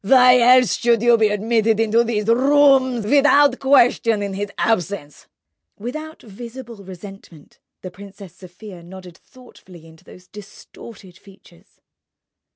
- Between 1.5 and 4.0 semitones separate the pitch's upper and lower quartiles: No, average, 4.5 semitones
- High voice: Yes, high, 215 Hz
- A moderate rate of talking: No, slow, 125 wpm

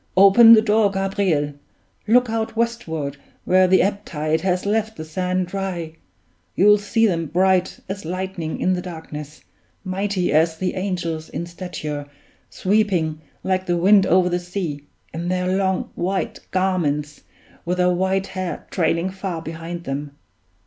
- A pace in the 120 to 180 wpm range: Yes, average, 150 wpm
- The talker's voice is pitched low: No, medium, 185 Hz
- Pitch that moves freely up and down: No, average, 2.9 semitones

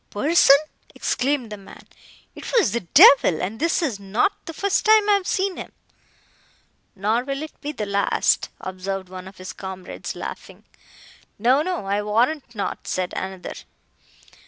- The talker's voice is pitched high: Yes, high, 225 Hz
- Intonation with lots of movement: Yes, wide, 7.9 semitones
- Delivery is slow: No, average, 155 wpm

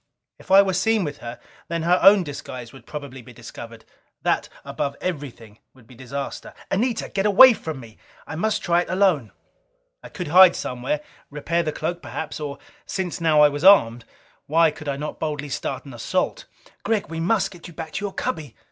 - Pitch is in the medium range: Yes, medium, 155 Hz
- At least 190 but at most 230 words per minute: Yes, average, 195 wpm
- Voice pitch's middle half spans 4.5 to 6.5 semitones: Yes, average, 5.2 semitones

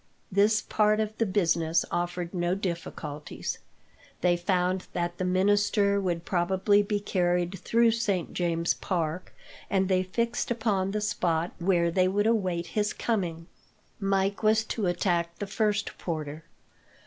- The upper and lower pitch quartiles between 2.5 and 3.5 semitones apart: Yes, average, 3.0 semitones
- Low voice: No, medium, 185 Hz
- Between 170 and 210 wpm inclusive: No, average, 140 wpm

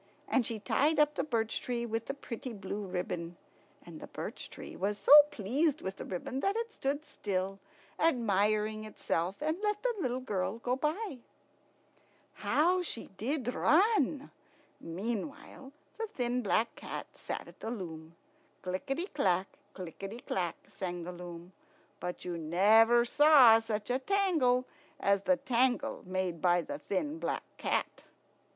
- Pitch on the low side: No, high, 230 Hz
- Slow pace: No, average, 150 wpm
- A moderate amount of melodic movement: No, wide, 6.9 semitones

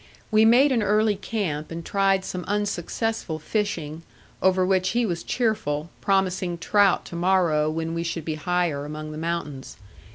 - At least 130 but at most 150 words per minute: No, average, 160 wpm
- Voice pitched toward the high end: No, medium, 180 Hz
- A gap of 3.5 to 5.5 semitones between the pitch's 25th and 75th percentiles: Yes, average, 4.2 semitones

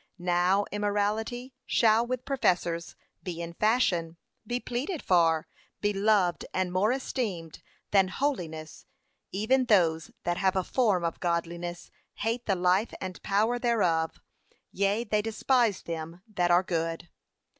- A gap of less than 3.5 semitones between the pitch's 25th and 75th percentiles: No, average, 4.4 semitones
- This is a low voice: No, high, 195 Hz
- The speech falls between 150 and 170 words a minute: No, slow, 135 wpm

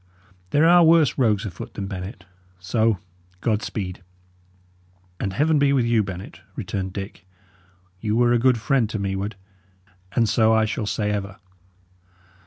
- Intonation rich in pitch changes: No, average, 3.7 semitones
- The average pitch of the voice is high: No, low, 110 Hz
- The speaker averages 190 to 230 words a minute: No, average, 155 wpm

